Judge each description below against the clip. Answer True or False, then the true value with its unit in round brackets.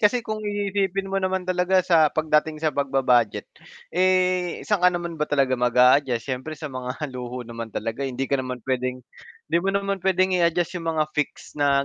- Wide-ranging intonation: True (6.3 semitones)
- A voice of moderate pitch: True (155 Hz)